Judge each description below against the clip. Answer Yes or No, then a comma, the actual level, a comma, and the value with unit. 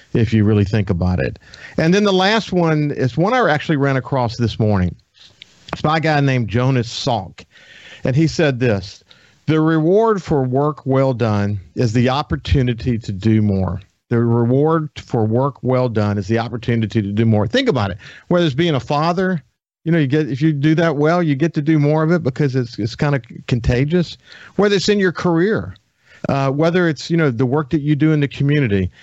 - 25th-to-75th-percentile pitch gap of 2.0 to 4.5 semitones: No, wide, 5.5 semitones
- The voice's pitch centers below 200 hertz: Yes, medium, 140 Hz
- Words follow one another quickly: Yes, fast, 210 wpm